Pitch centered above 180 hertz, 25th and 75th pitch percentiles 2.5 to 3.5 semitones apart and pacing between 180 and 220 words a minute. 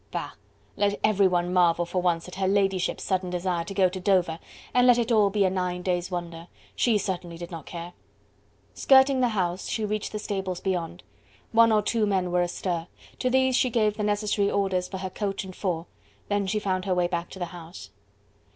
Yes: high, 190 Hz; average, 2.8 semitones; fast, 205 wpm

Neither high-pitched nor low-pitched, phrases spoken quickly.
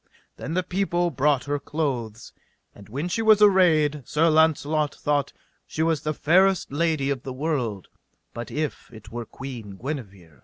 No: medium, 145 Hz; average, 160 wpm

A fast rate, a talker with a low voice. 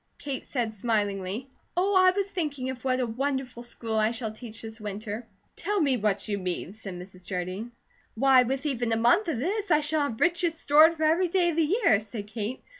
No: fast, 210 wpm; very high, 250 Hz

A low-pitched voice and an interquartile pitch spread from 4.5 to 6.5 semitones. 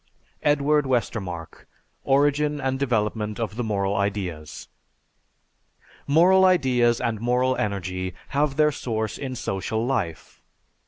Yes: low, 120 Hz; wide, 5.5 semitones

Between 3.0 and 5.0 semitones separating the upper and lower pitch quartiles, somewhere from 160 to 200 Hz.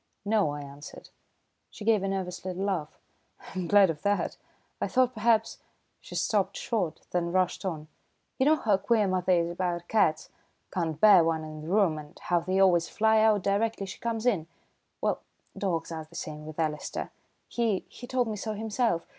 Yes: average, 4.6 semitones; medium, 185 Hz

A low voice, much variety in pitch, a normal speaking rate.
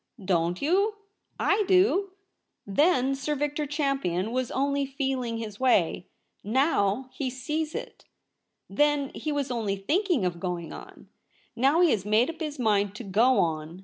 No: very high, 260 Hz; wide, 6.5 semitones; average, 155 wpm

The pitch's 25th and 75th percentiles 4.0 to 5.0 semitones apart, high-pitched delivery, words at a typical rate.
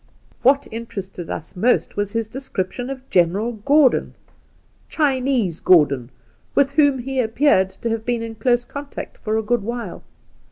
Yes: average, 4.7 semitones; high, 235 Hz; average, 160 wpm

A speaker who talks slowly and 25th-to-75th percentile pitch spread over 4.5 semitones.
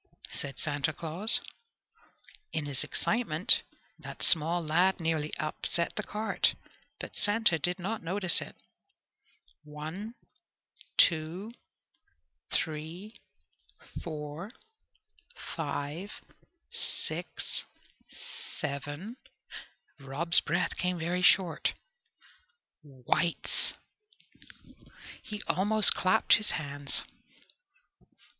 No: slow, 80 wpm; average, 4.1 semitones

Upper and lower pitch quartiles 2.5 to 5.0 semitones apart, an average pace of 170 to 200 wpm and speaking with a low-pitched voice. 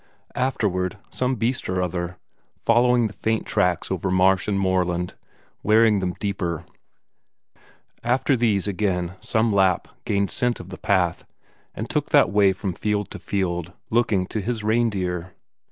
No: average, 3.3 semitones; average, 145 wpm; low, 100 Hz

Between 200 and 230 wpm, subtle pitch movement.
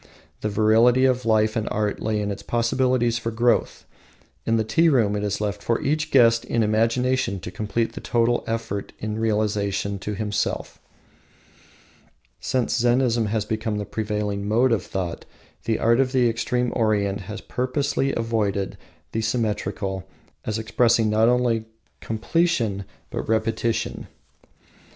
No: average, 145 wpm; narrow, 2.3 semitones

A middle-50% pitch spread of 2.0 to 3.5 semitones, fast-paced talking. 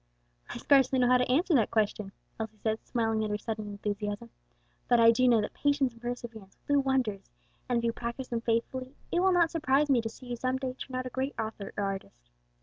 Yes: average, 3.2 semitones; fast, 235 wpm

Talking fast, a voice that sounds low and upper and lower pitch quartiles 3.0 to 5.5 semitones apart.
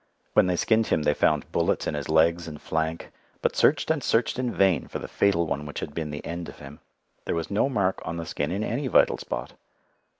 Yes: fast, 235 wpm; very low, 85 Hz; average, 5.0 semitones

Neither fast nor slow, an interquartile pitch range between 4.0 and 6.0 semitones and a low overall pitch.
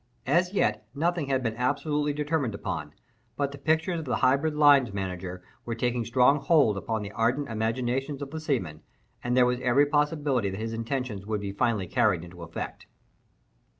Yes: average, 180 wpm; average, 5.0 semitones; low, 125 Hz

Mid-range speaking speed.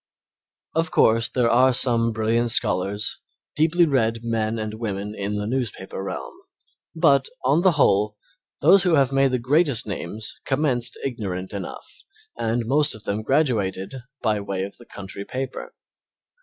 Yes: average, 150 wpm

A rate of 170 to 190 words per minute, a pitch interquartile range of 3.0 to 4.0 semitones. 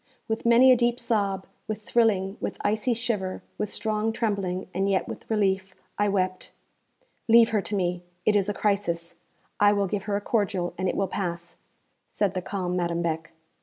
No: average, 185 wpm; narrow, 2.6 semitones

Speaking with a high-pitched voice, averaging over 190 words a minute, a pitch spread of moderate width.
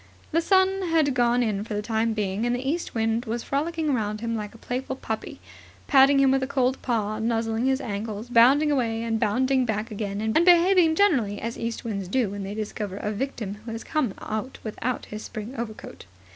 Yes: high, 230 Hz; fast, 205 wpm; average, 3.8 semitones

